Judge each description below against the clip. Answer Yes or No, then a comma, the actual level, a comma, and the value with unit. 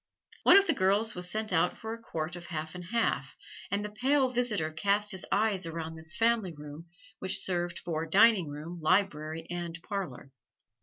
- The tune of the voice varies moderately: Yes, average, 4.6 semitones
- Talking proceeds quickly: No, average, 185 wpm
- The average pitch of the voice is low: No, medium, 180 Hz